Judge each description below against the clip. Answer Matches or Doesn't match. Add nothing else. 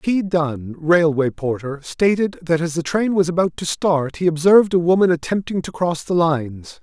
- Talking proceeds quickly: Doesn't match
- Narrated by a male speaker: Matches